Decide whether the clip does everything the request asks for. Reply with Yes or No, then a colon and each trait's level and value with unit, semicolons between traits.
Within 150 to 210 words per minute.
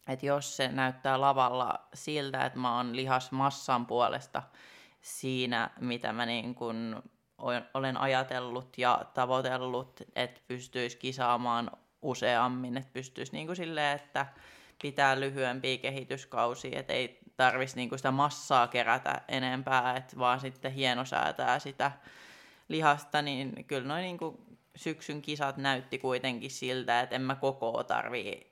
No: average, 125 wpm